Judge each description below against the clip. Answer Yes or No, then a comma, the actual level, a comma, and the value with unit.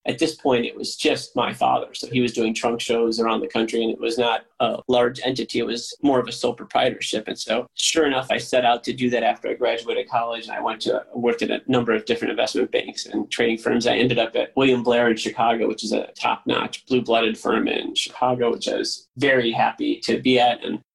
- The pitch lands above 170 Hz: No, low, 120 Hz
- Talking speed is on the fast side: Yes, fast, 245 wpm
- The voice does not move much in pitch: Yes, narrow, 1.6 semitones